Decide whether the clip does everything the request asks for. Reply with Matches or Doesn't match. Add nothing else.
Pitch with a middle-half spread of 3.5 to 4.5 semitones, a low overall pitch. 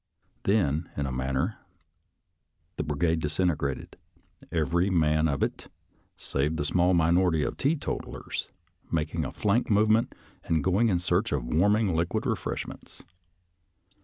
Matches